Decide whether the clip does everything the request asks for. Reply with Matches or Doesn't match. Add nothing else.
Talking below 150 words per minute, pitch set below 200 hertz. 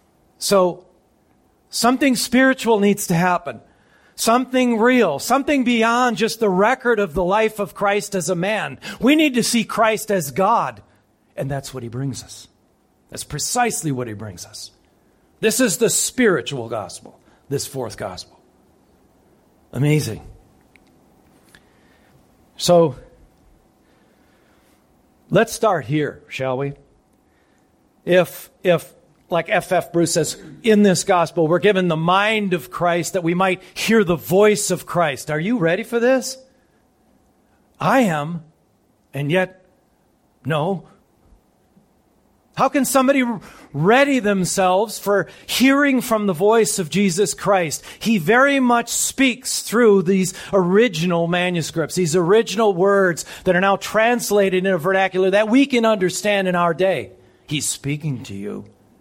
Matches